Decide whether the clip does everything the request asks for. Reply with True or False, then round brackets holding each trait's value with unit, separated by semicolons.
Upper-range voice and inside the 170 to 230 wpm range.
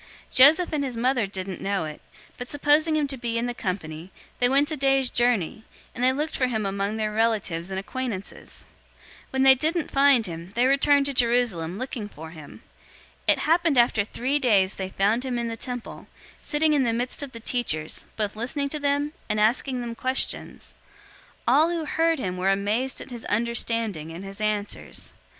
True (240 Hz; 200 wpm)